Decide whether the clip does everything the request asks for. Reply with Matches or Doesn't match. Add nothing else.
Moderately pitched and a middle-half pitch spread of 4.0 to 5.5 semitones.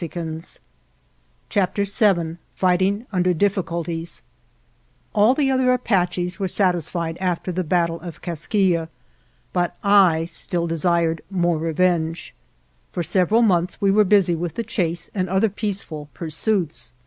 Doesn't match